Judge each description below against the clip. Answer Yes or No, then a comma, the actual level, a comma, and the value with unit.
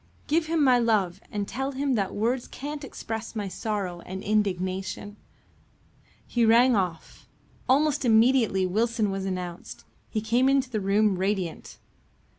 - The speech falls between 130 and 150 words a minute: Yes, average, 140 wpm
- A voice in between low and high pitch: No, high, 215 Hz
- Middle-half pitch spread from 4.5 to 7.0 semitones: Yes, average, 4.8 semitones